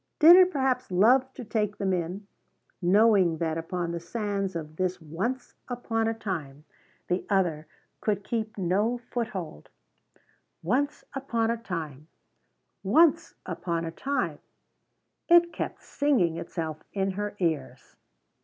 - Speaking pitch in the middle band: No, high, 195 Hz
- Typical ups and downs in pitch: No, wide, 5.9 semitones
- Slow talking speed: Yes, slow, 130 wpm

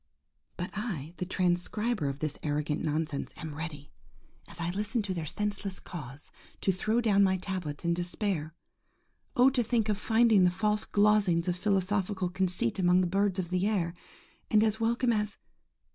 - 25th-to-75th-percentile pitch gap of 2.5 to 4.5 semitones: Yes, average, 3.7 semitones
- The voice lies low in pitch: No, medium, 185 Hz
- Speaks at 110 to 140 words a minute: No, average, 160 wpm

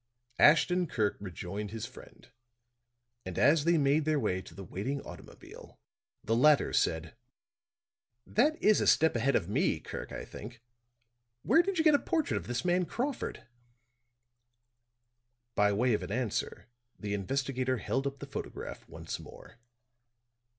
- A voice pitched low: Yes, low, 130 Hz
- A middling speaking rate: Yes, average, 150 wpm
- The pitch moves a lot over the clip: Yes, wide, 7.8 semitones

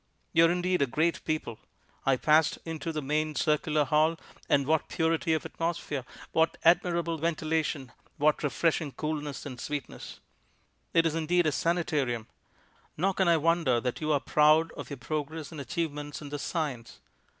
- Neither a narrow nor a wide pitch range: No, narrow, 2.3 semitones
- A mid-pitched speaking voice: Yes, medium, 155 Hz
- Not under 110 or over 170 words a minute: Yes, average, 160 wpm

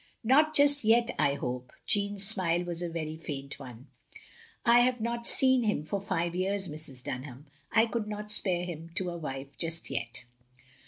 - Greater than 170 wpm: Yes, average, 190 wpm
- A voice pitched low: No, medium, 180 Hz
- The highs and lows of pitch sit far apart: Yes, wide, 6.7 semitones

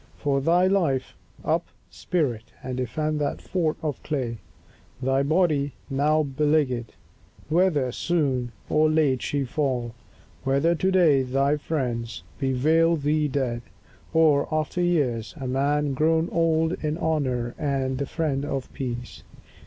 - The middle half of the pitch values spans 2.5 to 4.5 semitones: Yes, average, 3.3 semitones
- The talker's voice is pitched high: No, medium, 145 Hz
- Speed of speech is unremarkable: No, slow, 130 wpm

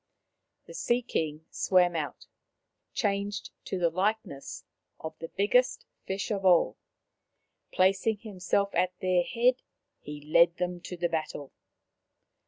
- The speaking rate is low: Yes, slow, 125 wpm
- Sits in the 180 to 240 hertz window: Yes, medium, 185 Hz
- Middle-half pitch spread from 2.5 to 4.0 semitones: Yes, average, 3.1 semitones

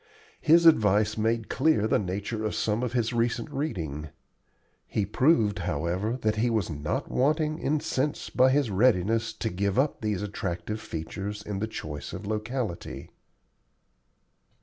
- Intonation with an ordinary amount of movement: Yes, average, 4.4 semitones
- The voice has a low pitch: Yes, low, 110 Hz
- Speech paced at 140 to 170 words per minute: Yes, average, 150 wpm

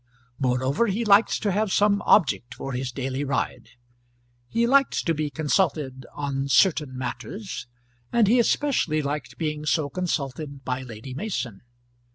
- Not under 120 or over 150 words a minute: Yes, average, 145 wpm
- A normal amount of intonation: No, wide, 7.2 semitones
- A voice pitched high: No, medium, 150 Hz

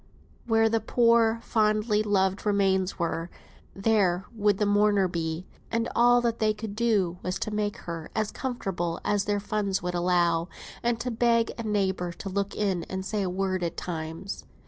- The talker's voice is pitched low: No, high, 200 Hz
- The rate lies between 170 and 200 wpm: Yes, average, 175 wpm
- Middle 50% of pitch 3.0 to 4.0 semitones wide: Yes, average, 3.3 semitones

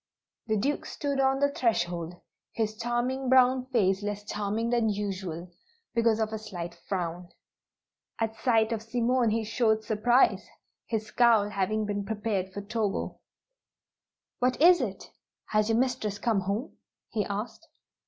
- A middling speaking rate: Yes, average, 145 wpm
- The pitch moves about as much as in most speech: Yes, average, 3.0 semitones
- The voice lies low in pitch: No, high, 220 Hz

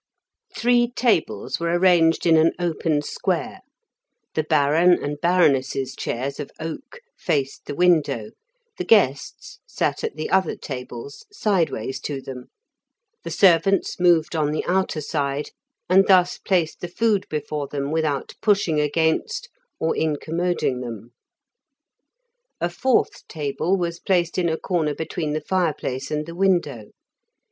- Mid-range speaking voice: Yes, medium, 160 Hz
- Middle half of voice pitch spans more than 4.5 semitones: No, average, 3.8 semitones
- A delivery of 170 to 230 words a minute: No, slow, 135 wpm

